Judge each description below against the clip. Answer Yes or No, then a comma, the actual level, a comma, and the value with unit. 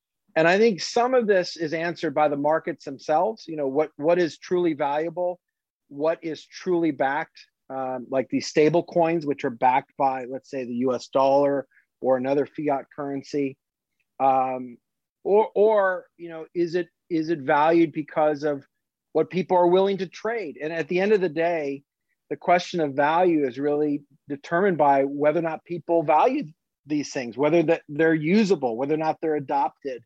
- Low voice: No, medium, 155 Hz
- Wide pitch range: No, average, 3.5 semitones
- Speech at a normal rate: Yes, average, 180 wpm